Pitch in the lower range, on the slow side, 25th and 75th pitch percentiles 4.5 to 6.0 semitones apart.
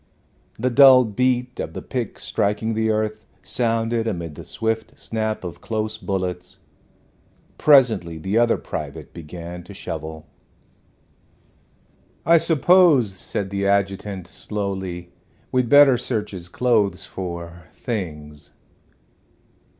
Yes: low, 105 Hz; slow, 110 wpm; average, 4.8 semitones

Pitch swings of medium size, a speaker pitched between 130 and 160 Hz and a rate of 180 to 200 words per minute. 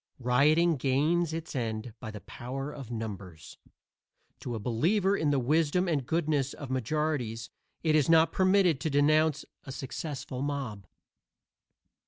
No: average, 4.3 semitones; medium, 140 Hz; average, 140 wpm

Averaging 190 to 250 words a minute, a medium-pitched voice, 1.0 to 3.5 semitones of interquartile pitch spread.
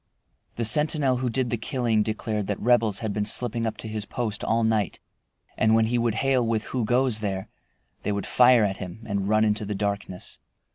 No: fast, 205 wpm; low, 110 Hz; narrow, 2.6 semitones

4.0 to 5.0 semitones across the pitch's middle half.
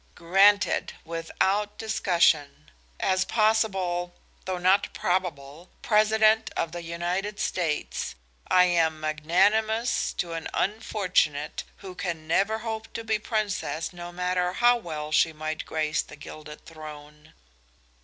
Yes: average, 4.7 semitones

